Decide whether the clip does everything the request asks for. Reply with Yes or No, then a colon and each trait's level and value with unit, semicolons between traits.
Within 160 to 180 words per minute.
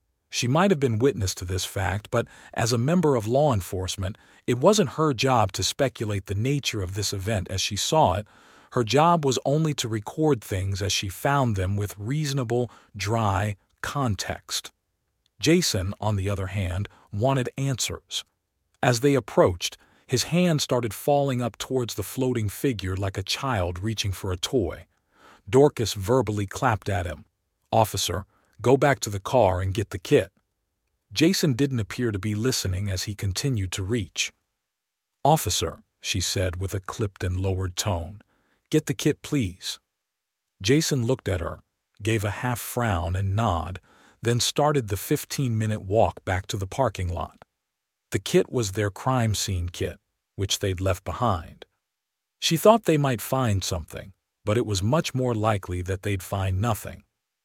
Yes: average, 165 wpm